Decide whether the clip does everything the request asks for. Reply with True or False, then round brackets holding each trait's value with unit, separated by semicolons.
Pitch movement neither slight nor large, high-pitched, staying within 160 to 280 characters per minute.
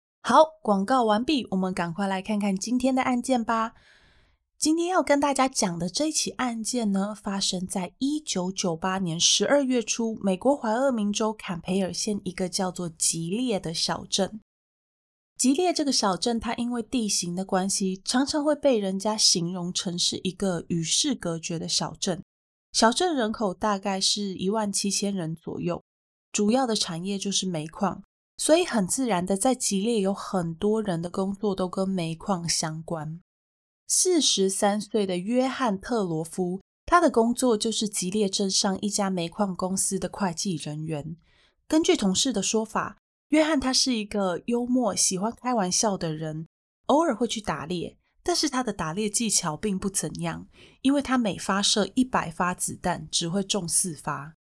True (4.5 semitones; 200 Hz; 250 characters per minute)